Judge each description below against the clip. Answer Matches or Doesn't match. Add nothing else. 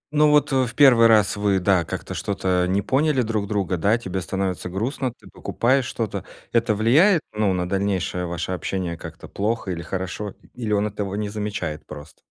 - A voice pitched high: Doesn't match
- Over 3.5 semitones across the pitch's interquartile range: Matches